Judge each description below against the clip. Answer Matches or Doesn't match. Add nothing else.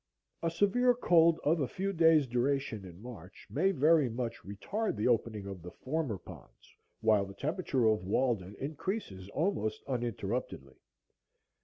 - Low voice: Matches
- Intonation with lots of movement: Matches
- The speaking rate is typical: Matches